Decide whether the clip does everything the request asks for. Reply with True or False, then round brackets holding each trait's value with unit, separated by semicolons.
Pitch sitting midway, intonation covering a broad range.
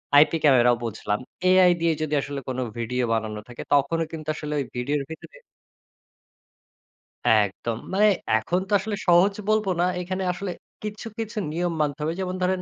True (155 Hz; 6.7 semitones)